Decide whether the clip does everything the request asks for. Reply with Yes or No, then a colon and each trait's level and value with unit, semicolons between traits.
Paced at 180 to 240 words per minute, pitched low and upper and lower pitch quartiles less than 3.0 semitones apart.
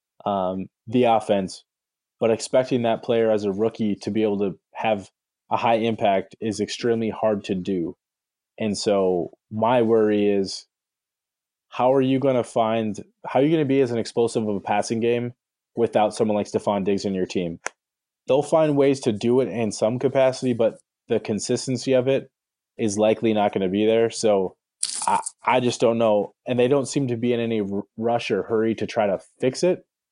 No: average, 195 wpm; low, 115 Hz; average, 3.4 semitones